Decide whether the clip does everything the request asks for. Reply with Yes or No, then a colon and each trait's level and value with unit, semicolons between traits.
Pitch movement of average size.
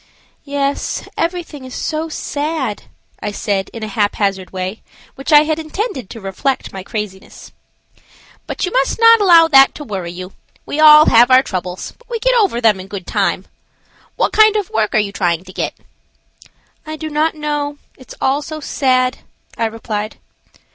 No: wide, 7.2 semitones